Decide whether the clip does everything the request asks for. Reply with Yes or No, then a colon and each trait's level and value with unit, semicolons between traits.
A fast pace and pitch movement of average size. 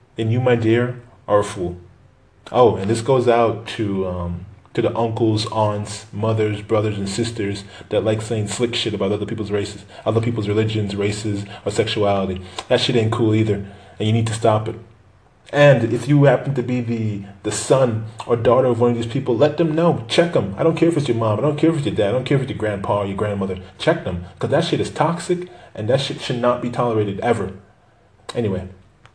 Yes: fast, 225 wpm; average, 3.1 semitones